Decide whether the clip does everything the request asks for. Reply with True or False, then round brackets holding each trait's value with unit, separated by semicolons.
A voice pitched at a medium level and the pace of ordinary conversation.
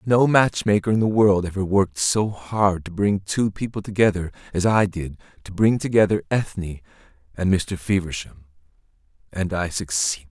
False (95 Hz; 165 wpm)